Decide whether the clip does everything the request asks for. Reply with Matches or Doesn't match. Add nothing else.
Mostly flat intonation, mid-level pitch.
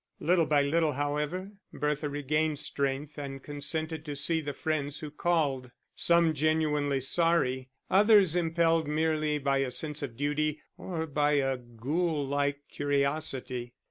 Matches